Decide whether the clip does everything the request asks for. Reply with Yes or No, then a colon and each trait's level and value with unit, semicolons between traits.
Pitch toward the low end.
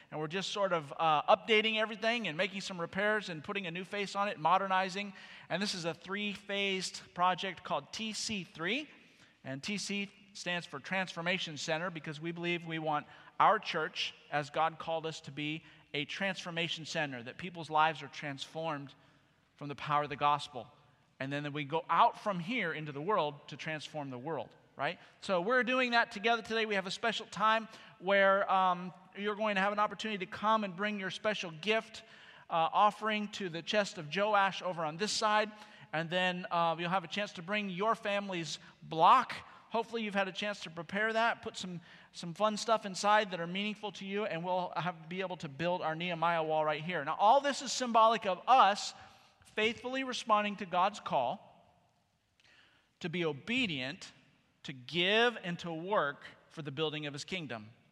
No: medium, 185 Hz